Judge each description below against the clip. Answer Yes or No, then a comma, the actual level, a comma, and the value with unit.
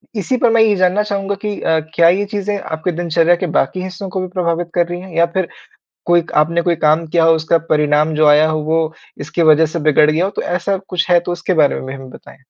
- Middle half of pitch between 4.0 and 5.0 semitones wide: No, average, 2.8 semitones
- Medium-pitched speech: Yes, medium, 170 Hz